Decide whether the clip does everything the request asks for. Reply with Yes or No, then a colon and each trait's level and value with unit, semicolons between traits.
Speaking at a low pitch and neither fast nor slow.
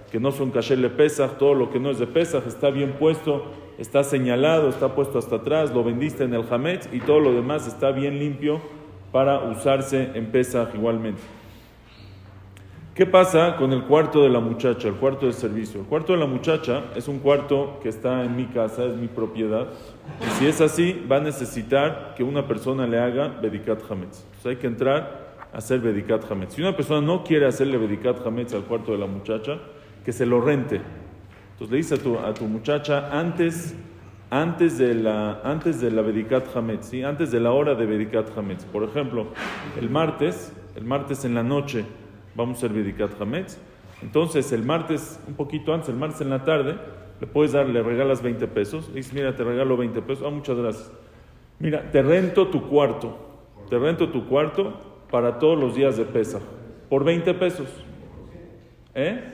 Yes: low, 130 Hz; average, 195 wpm